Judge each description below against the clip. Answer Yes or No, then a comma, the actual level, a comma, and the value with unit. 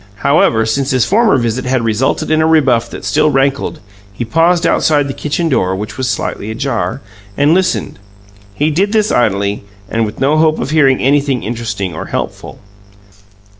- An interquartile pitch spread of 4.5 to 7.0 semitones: Yes, average, 5.3 semitones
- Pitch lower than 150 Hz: Yes, low, 135 Hz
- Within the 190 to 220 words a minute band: No, average, 170 wpm